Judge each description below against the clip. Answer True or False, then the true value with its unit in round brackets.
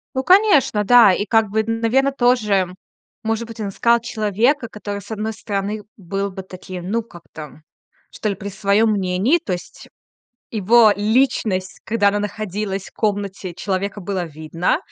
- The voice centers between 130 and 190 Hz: False (210 Hz)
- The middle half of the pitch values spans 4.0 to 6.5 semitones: False (2.8 semitones)